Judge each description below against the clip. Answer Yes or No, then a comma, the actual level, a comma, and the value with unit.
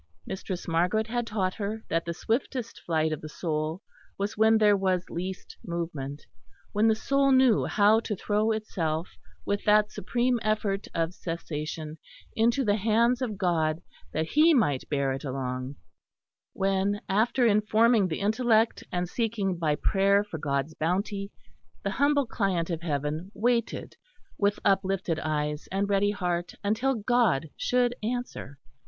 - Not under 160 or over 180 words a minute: No, average, 150 wpm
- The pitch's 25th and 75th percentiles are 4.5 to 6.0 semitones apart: Yes, average, 5.1 semitones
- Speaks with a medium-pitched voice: No, high, 195 Hz